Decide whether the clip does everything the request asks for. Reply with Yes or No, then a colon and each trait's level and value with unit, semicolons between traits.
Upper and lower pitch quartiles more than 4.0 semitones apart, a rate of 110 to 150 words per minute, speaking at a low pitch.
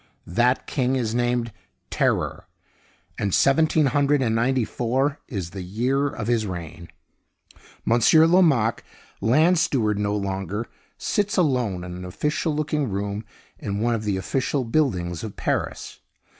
Yes: wide, 5.5 semitones; average, 140 wpm; low, 120 Hz